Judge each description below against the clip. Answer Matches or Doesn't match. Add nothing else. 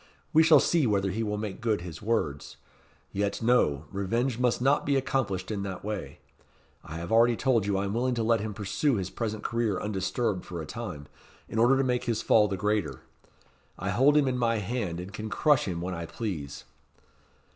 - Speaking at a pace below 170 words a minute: Doesn't match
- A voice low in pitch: Matches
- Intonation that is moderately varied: Matches